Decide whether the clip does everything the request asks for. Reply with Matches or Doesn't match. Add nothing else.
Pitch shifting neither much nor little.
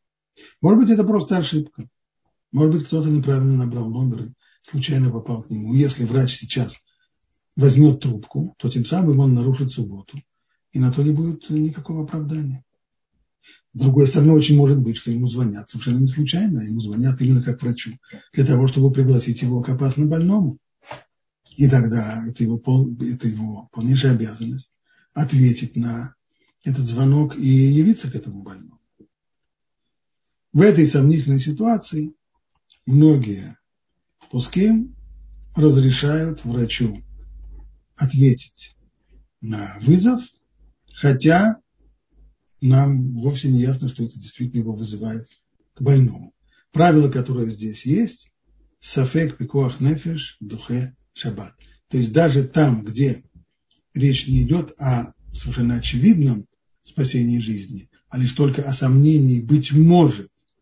Matches